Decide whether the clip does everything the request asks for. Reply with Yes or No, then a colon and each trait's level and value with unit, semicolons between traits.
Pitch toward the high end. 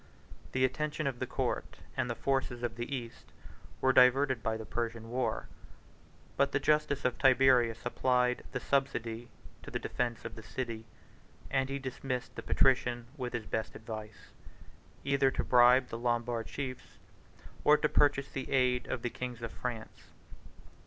No: low, 125 Hz